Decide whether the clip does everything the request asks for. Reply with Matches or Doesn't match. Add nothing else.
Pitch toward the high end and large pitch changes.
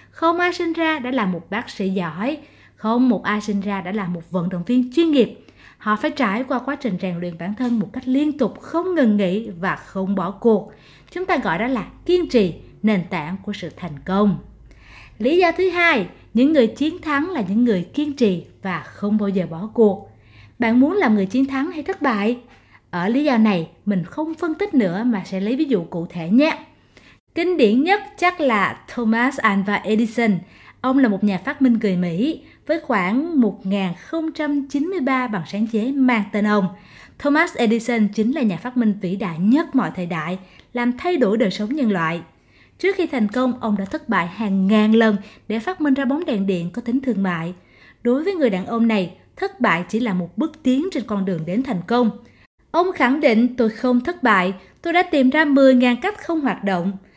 Matches